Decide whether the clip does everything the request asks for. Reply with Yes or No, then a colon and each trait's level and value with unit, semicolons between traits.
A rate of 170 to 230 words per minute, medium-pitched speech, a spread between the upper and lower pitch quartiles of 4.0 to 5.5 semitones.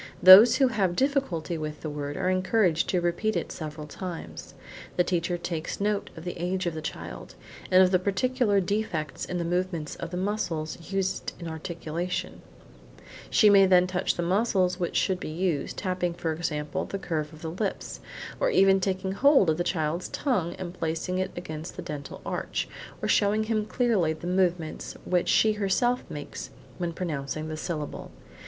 No: average, 180 wpm; medium, 180 Hz; average, 3.2 semitones